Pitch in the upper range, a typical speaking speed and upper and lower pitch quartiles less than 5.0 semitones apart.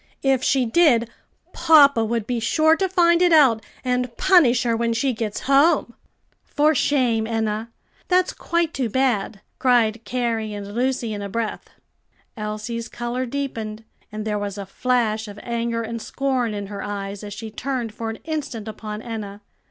Yes: high, 235 Hz; average, 165 wpm; average, 3.6 semitones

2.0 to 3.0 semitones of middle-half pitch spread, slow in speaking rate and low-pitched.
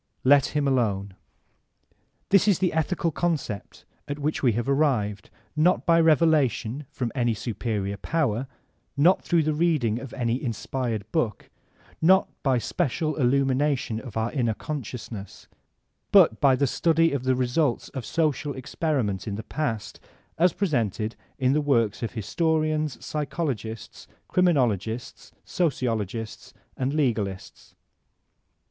No: wide, 5.4 semitones; slow, 130 wpm; low, 130 Hz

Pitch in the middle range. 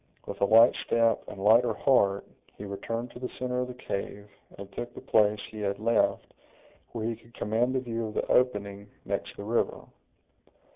No: low, 115 Hz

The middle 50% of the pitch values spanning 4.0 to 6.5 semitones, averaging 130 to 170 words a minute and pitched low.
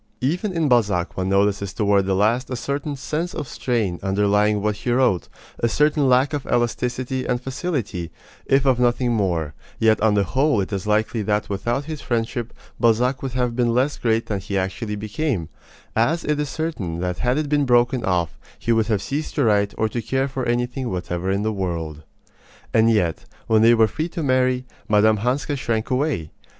No: average, 4.4 semitones; average, 195 wpm; low, 115 Hz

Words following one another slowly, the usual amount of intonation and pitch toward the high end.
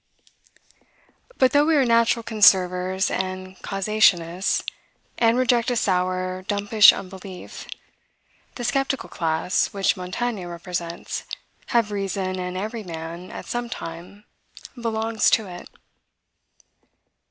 Yes: slow, 105 wpm; average, 4.0 semitones; high, 195 Hz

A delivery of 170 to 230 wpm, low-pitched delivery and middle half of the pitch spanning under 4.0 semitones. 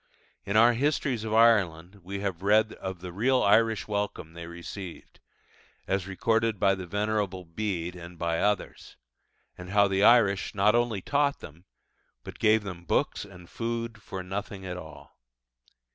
No: average, 160 wpm; low, 100 Hz; average, 3.4 semitones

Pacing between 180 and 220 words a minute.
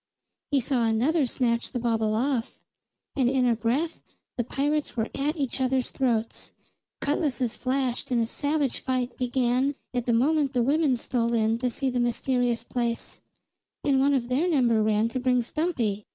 No: average, 170 wpm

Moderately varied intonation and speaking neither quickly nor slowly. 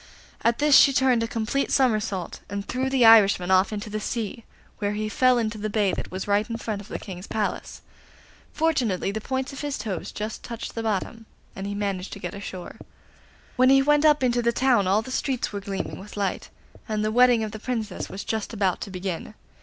No: average, 3.6 semitones; fast, 215 wpm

